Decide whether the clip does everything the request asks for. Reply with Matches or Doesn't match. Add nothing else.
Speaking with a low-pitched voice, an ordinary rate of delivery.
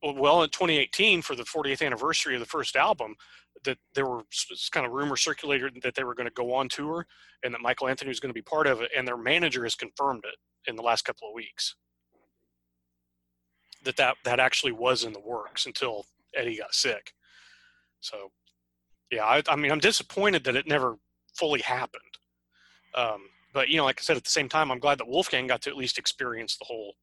Doesn't match